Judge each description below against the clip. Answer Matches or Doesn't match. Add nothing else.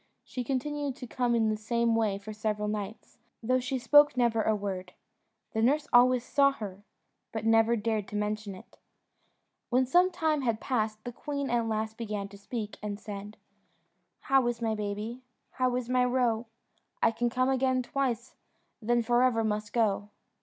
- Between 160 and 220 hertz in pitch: Doesn't match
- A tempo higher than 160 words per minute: Matches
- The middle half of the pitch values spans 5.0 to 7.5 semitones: Doesn't match